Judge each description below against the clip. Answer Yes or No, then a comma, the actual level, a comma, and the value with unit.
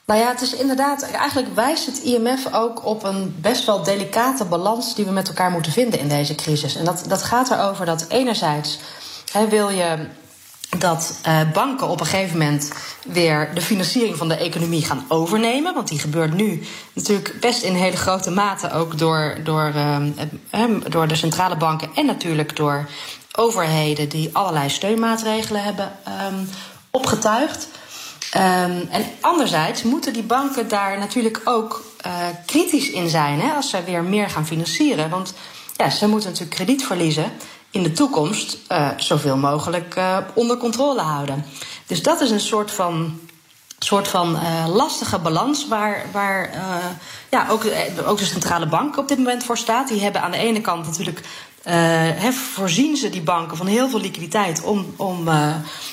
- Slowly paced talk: No, average, 165 wpm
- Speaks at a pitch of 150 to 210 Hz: Yes, high, 190 Hz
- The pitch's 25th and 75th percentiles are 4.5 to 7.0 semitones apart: Yes, wide, 5.5 semitones